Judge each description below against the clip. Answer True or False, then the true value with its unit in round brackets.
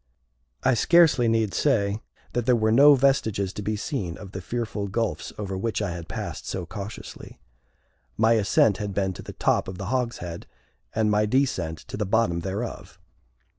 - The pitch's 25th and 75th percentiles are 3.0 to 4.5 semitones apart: True (3.3 semitones)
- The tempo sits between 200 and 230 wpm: False (175 wpm)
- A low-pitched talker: True (105 Hz)